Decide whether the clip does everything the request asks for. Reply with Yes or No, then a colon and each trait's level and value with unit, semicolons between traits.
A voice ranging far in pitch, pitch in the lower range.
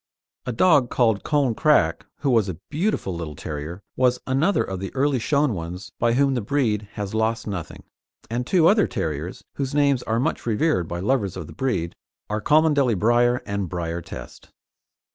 Yes: wide, 6.4 semitones; low, 115 Hz